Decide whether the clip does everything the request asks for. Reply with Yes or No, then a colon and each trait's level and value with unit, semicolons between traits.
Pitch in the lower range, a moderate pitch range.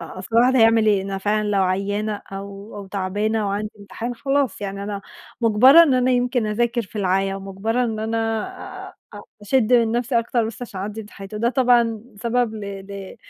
No: high, 215 Hz; average, 3.0 semitones